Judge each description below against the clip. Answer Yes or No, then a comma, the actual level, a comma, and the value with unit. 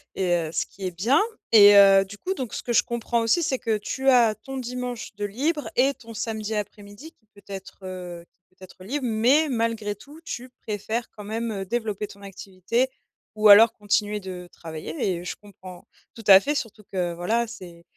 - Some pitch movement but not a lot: Yes, average, 3.6 semitones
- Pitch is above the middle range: Yes, high, 210 Hz